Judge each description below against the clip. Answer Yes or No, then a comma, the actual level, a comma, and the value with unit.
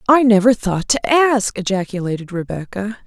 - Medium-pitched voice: No, high, 210 Hz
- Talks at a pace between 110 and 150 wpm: Yes, slow, 135 wpm